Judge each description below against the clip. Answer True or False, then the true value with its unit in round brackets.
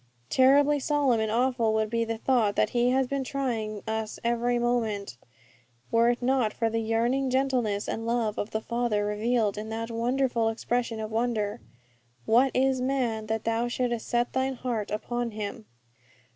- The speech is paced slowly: False (170 wpm)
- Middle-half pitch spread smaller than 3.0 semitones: True (2.4 semitones)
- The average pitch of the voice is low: False (235 Hz)